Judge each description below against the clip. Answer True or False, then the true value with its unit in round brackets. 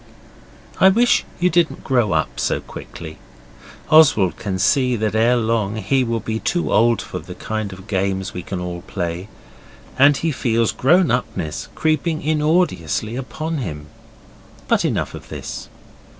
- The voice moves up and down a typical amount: False (7.7 semitones)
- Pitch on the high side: False (115 Hz)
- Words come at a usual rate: True (150 wpm)